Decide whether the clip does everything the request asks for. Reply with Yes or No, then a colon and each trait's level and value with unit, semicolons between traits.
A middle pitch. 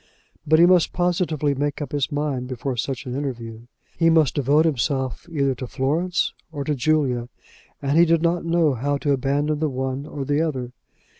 Yes: medium, 145 Hz